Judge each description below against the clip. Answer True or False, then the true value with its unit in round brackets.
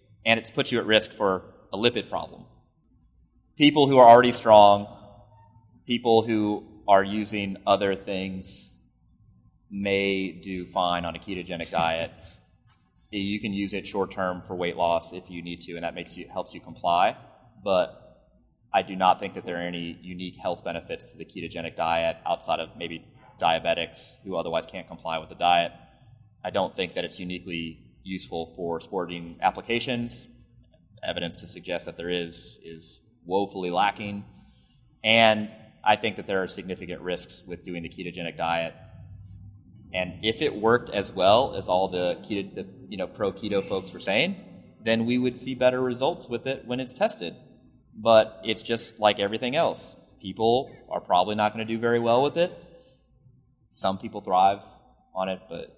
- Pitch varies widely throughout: False (4.5 semitones)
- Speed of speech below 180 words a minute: True (170 wpm)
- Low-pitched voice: True (100 Hz)